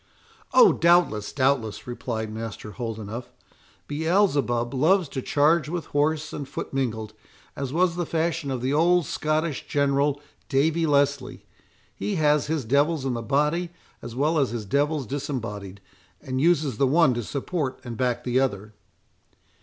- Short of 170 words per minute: Yes, average, 150 wpm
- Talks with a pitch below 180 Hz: Yes, medium, 140 Hz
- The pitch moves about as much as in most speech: Yes, average, 4.5 semitones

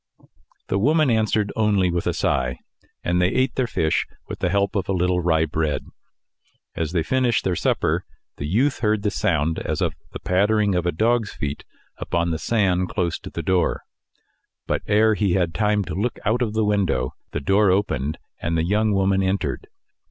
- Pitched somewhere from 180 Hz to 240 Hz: No, very low, 95 Hz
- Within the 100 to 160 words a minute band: No, average, 190 wpm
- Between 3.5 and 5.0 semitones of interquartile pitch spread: Yes, average, 3.8 semitones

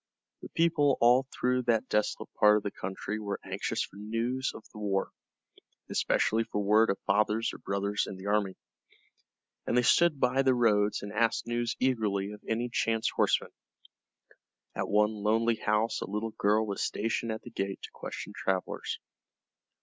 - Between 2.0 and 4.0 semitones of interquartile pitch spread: Yes, narrow, 2.5 semitones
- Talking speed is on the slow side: No, average, 170 wpm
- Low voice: Yes, low, 110 Hz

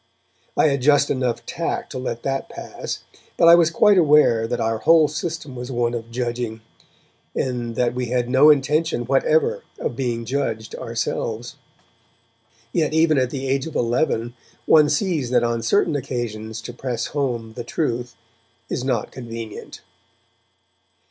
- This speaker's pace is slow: No, average, 155 wpm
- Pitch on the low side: Yes, low, 125 Hz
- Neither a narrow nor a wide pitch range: Yes, average, 3.8 semitones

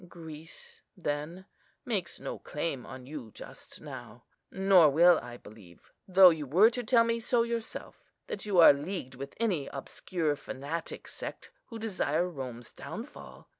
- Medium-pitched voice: Yes, medium, 165 Hz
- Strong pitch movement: Yes, wide, 5.9 semitones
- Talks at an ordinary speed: Yes, average, 150 wpm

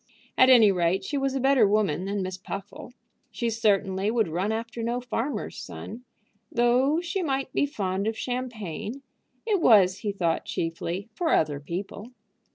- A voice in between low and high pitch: No, high, 220 Hz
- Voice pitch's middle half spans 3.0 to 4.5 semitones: No, average, 5.0 semitones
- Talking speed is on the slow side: No, average, 165 wpm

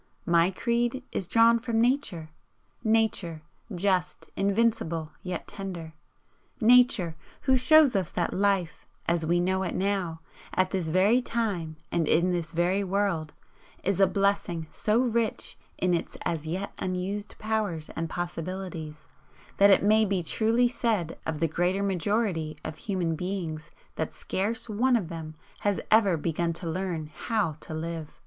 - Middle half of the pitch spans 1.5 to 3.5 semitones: No, average, 4.4 semitones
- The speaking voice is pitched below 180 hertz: No, medium, 185 Hz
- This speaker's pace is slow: No, average, 150 wpm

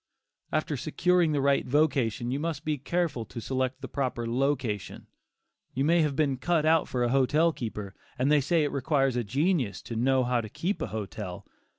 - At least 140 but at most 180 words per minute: No, average, 195 wpm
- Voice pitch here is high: No, low, 135 Hz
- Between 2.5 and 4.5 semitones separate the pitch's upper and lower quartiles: Yes, average, 4.2 semitones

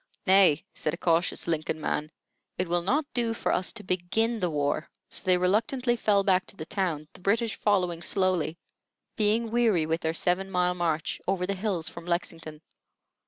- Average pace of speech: Yes, average, 180 wpm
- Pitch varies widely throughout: No, average, 3.6 semitones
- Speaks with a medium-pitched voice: Yes, medium, 180 Hz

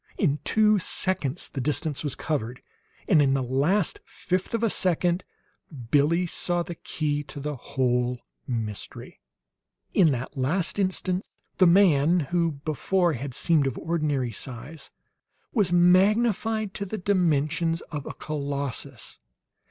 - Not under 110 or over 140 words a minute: Yes, slow, 135 wpm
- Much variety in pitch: No, average, 4.8 semitones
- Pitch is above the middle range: No, medium, 160 Hz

